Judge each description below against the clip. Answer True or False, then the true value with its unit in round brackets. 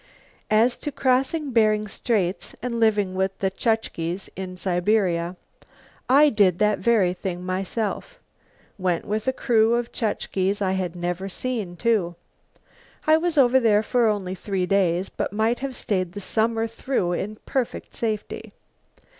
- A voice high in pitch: True (210 Hz)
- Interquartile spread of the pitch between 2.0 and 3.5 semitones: False (3.9 semitones)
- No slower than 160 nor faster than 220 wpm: False (145 wpm)